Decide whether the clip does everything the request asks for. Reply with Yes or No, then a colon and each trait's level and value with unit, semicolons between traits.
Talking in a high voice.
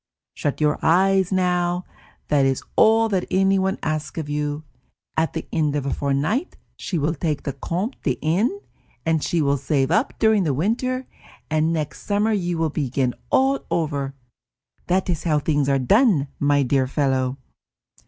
No: medium, 160 Hz